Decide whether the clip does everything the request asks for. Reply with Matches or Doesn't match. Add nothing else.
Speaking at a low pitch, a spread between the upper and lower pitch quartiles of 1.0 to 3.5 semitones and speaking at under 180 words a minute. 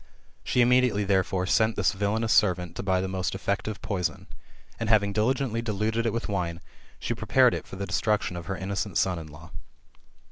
Doesn't match